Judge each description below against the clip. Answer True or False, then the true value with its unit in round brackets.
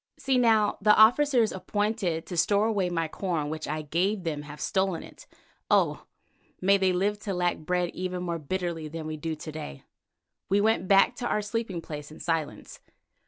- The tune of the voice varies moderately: True (4.3 semitones)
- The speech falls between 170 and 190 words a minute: True (185 wpm)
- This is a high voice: False (180 Hz)